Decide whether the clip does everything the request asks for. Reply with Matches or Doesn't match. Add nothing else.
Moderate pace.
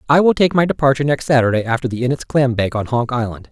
Doesn't match